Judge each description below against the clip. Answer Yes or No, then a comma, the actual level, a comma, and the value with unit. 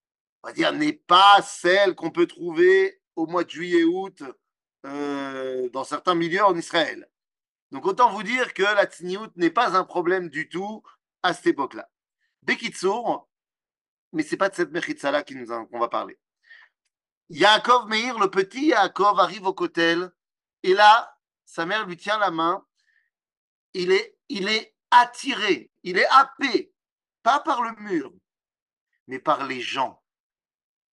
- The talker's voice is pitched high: Yes, high, 205 Hz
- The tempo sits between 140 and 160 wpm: Yes, average, 155 wpm